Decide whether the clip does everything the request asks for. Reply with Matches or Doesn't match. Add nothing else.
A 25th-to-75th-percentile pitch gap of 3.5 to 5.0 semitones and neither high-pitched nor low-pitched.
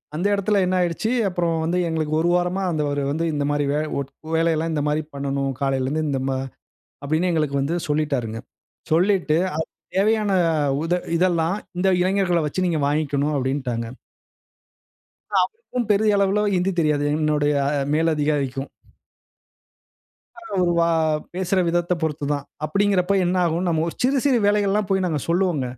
Matches